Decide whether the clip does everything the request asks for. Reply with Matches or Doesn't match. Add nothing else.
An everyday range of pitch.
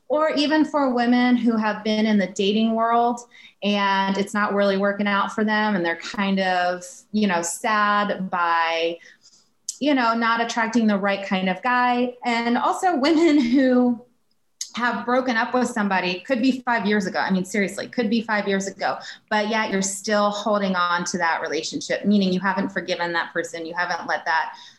Matches